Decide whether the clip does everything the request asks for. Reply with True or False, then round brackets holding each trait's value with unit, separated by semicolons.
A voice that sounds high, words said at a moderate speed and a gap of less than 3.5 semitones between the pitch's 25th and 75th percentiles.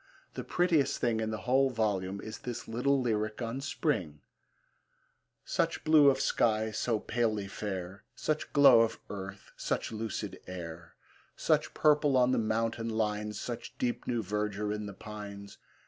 False (110 Hz; 150 wpm; 3.1 semitones)